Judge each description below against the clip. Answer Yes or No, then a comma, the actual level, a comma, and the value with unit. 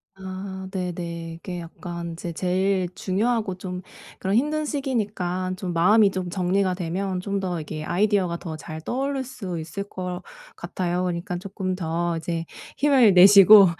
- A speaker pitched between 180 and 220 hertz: Yes, medium, 185 Hz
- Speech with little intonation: Yes, narrow, 2.3 semitones